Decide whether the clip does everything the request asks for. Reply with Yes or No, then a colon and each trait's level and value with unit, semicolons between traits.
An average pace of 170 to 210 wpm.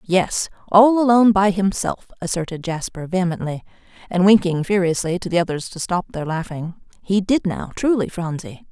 No: average, 160 wpm